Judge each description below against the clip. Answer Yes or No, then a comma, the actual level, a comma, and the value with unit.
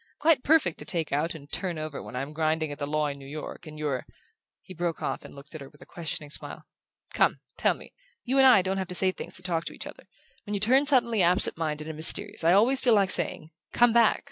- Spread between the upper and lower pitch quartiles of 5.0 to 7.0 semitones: Yes, average, 5.3 semitones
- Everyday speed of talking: No, fast, 255 wpm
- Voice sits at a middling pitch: Yes, medium, 170 Hz